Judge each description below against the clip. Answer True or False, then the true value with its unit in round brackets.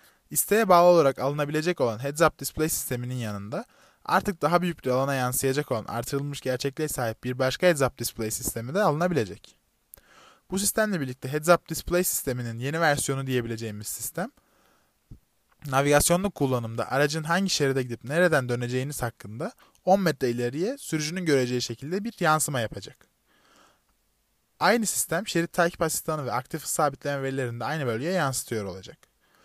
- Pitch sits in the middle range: True (145 Hz)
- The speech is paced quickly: True (145 wpm)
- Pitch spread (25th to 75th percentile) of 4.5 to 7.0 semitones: True (5.4 semitones)